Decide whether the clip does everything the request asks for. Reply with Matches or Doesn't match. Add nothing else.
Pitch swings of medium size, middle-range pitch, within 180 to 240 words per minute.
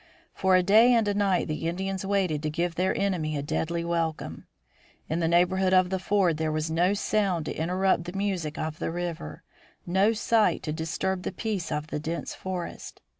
Matches